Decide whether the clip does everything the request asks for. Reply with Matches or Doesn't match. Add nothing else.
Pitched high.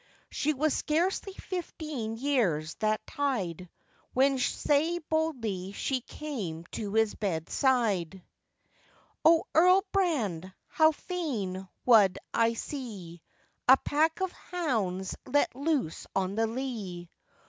Matches